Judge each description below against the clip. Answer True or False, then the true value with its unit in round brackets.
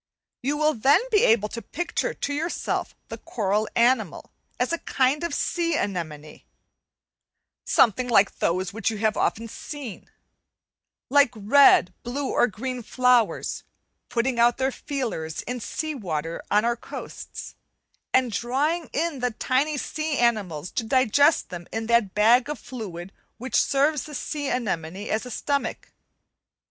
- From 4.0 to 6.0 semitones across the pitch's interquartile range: True (5.1 semitones)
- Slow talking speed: False (145 wpm)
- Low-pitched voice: False (240 Hz)